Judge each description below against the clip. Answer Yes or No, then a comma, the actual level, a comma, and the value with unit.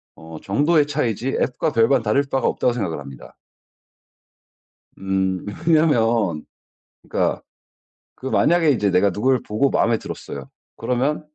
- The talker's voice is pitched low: Yes, low, 120 Hz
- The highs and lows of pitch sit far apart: Yes, wide, 6.3 semitones